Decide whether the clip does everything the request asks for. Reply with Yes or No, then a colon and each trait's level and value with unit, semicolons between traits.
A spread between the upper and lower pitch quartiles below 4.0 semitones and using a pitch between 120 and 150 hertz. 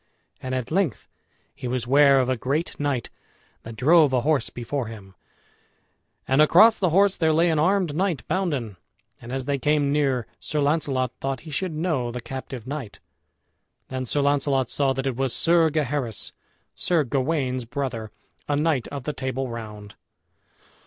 Yes: average, 3.4 semitones; medium, 140 Hz